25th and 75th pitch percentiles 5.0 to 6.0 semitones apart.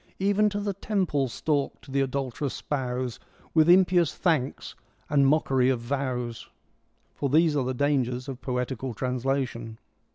No: average, 3.7 semitones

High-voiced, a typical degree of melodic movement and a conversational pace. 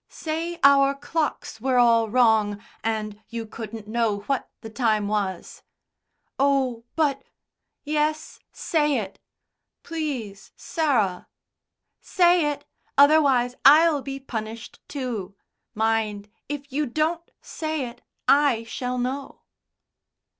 No: very high, 255 Hz; average, 4.9 semitones; slow, 110 wpm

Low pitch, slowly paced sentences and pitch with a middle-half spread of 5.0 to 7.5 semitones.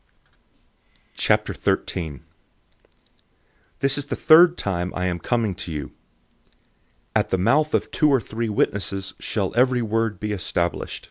Yes: low, 105 Hz; slow, 125 wpm; wide, 5.6 semitones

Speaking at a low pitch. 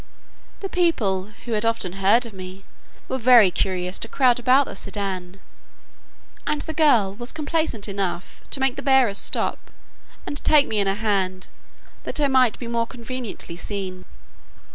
No: high, 225 Hz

